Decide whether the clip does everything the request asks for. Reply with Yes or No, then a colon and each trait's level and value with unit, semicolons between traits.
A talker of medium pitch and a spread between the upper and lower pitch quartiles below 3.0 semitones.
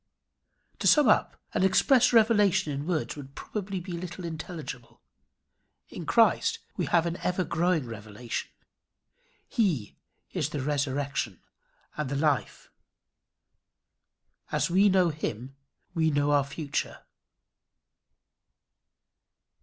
No: medium, 160 Hz; average, 4.7 semitones